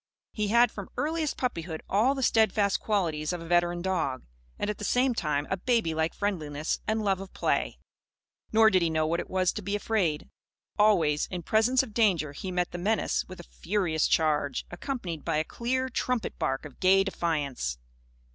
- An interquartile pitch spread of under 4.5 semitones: No, average, 5.3 semitones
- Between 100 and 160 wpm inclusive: No, average, 185 wpm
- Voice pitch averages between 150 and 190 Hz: Yes, medium, 185 Hz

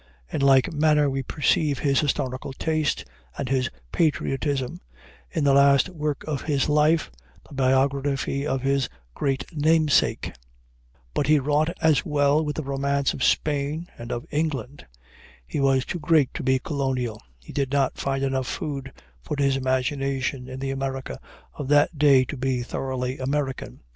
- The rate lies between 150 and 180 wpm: Yes, average, 160 wpm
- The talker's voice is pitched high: No, medium, 140 Hz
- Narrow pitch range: Yes, narrow, 1.9 semitones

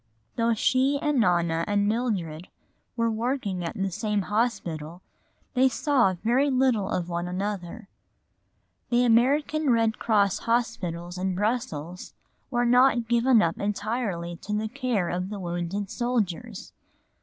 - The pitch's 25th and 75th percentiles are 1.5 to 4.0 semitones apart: No, average, 5.1 semitones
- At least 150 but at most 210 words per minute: No, slow, 135 wpm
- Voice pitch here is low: No, high, 215 Hz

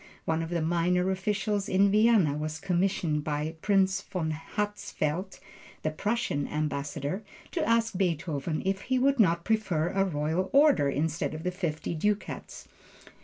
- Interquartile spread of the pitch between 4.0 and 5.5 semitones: Yes, average, 4.3 semitones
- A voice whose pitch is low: No, medium, 180 Hz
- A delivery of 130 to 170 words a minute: Yes, average, 145 wpm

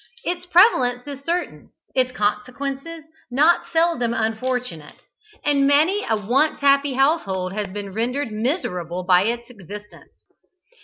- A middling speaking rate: No, slow, 120 wpm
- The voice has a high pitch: Yes, very high, 250 Hz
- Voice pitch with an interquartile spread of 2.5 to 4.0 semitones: No, wide, 5.6 semitones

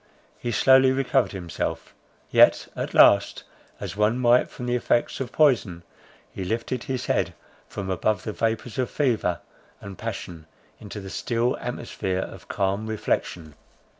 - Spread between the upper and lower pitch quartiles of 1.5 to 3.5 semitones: No, average, 4.3 semitones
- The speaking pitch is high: No, low, 110 Hz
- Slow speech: No, average, 145 wpm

